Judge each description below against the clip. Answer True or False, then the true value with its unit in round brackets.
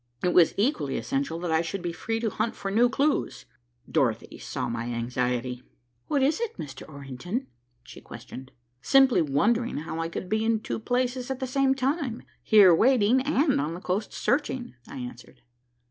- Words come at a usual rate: True (175 wpm)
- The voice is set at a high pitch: True (205 Hz)